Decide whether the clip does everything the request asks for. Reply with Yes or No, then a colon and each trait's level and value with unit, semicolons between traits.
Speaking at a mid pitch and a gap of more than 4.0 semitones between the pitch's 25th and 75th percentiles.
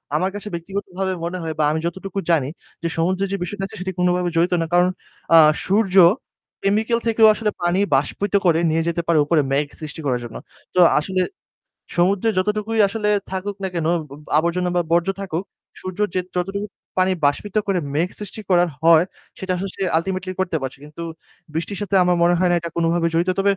No: medium, 180 Hz; average, 2.7 semitones